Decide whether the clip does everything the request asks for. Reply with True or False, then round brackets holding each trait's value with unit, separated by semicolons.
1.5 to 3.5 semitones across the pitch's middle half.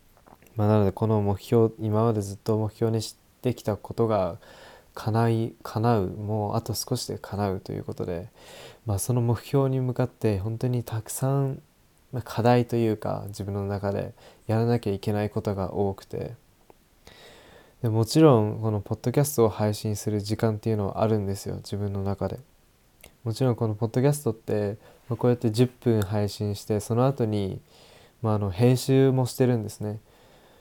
True (2.6 semitones)